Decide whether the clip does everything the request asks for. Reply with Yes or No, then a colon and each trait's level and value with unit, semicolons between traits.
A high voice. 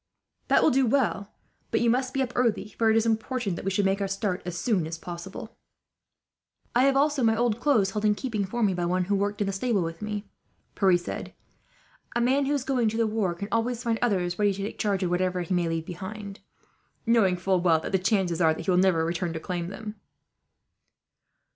Yes: high, 200 Hz